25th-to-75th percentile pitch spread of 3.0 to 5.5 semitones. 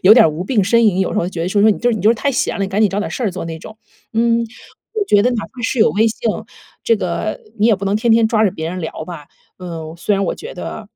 Yes: average, 3.9 semitones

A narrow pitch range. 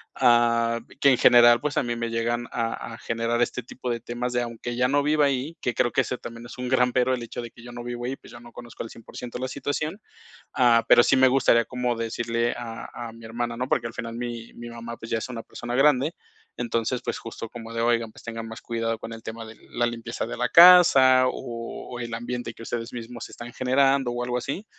Yes: narrow, 1.4 semitones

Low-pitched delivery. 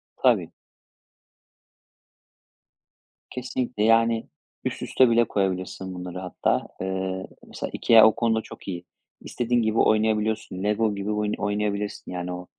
Yes: low, 105 Hz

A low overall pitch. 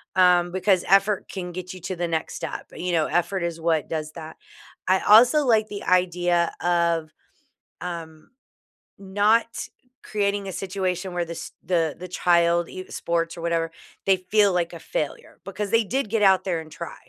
No: medium, 180 Hz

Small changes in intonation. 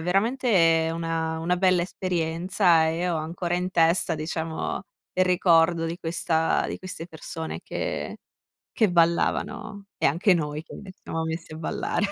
Yes: narrow, 2.1 semitones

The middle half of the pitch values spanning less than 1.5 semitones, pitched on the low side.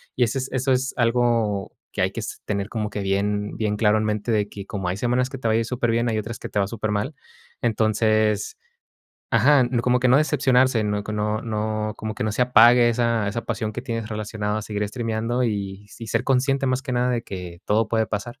No: average, 2.7 semitones; low, 110 Hz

